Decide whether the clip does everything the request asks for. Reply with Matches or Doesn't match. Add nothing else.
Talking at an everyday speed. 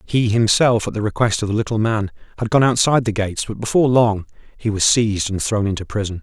Doesn't match